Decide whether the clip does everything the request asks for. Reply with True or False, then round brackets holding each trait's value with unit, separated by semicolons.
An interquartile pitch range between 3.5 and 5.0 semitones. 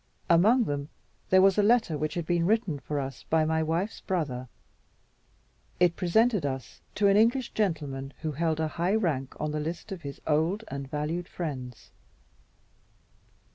True (4.7 semitones)